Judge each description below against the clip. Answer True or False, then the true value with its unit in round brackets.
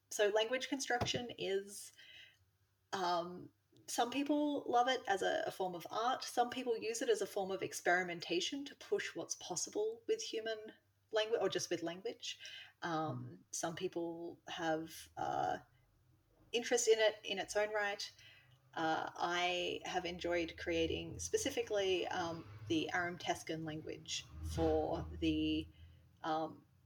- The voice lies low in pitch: False (175 Hz)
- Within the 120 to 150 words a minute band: True (135 wpm)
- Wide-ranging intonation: True (7.2 semitones)